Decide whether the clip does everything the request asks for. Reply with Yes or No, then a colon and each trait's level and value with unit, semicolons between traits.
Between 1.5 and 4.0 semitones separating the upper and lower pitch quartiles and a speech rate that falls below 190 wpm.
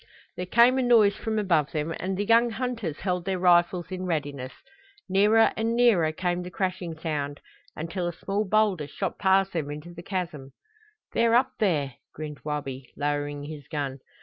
No: average, 5.3 semitones; average, 175 wpm